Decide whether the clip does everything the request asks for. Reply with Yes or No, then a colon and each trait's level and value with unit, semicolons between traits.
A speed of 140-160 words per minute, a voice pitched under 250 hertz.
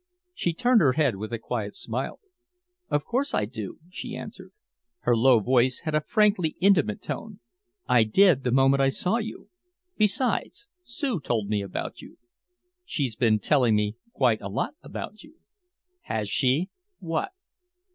Yes: average, 155 wpm; low, 135 Hz